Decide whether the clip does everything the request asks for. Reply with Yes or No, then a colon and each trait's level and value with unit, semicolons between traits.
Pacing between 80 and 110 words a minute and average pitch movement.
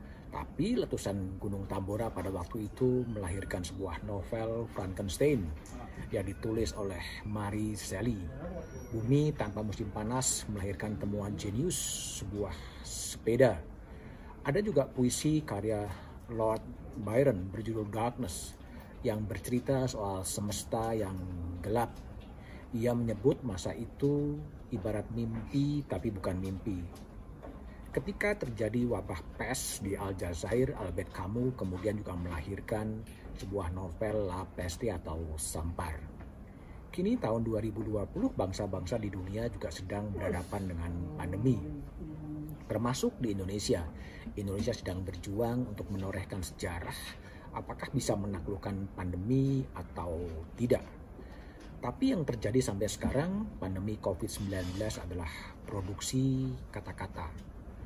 Yes: average, 105 wpm; average, 4.1 semitones